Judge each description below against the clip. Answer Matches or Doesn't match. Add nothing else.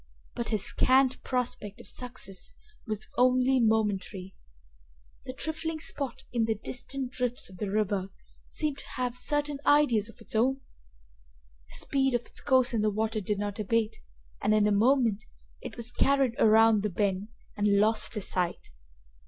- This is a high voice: Matches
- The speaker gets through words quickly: Doesn't match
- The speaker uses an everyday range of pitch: Matches